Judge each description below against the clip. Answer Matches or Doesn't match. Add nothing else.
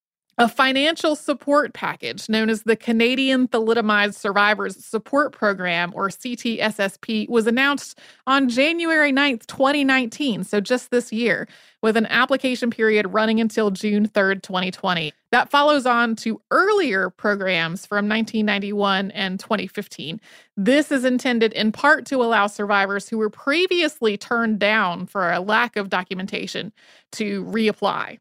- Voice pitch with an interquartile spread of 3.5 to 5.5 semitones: Matches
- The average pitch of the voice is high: Matches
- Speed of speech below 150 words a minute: Matches